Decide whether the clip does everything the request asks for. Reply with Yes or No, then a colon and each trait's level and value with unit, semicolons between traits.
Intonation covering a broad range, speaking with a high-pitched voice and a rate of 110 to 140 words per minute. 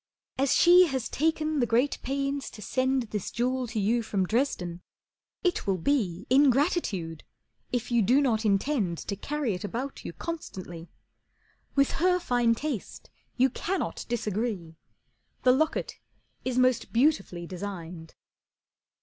Yes: wide, 6.0 semitones; high, 245 Hz; slow, 135 wpm